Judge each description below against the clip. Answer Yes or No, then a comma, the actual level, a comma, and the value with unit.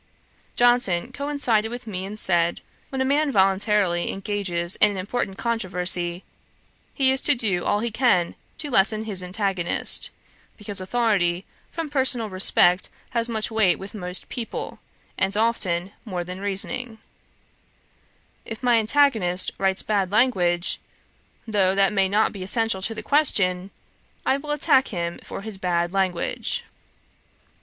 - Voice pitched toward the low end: No, high, 205 Hz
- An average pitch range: Yes, average, 4.2 semitones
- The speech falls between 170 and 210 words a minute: No, average, 140 wpm